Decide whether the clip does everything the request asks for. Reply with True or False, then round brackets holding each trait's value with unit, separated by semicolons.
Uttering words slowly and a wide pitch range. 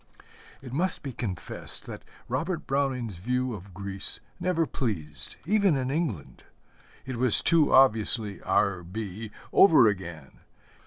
True (125 wpm; 6.1 semitones)